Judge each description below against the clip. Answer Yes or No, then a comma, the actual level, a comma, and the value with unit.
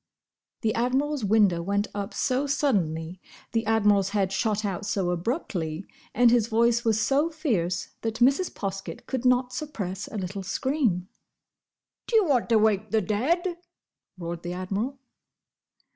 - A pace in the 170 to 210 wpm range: No, average, 145 wpm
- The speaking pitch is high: Yes, high, 215 Hz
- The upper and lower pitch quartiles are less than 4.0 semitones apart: No, average, 4.8 semitones